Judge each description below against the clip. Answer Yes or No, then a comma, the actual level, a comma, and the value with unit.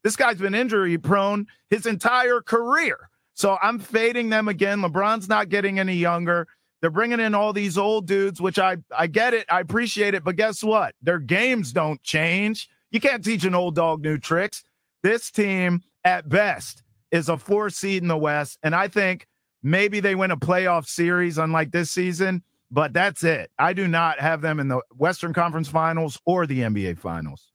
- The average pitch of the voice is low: No, medium, 185 Hz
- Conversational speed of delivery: Yes, average, 190 wpm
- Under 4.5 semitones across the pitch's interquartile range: Yes, average, 4.1 semitones